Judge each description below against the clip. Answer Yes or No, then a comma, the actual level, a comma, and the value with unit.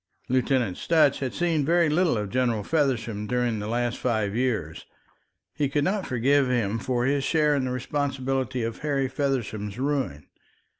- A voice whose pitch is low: Yes, low, 130 Hz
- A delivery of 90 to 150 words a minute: No, average, 160 wpm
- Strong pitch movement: No, average, 3.7 semitones